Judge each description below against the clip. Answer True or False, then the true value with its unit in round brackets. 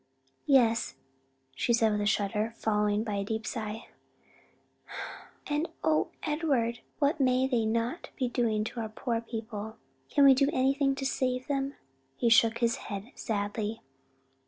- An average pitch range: True (3.5 semitones)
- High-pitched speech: True (230 Hz)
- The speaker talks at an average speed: True (150 wpm)